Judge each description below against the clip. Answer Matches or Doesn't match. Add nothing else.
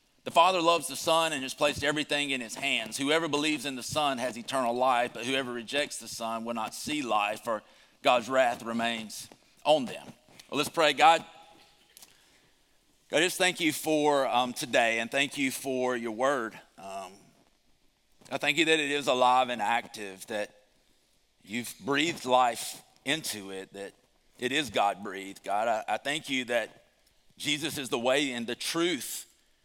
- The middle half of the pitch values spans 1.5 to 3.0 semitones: Doesn't match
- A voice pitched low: Matches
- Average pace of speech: Matches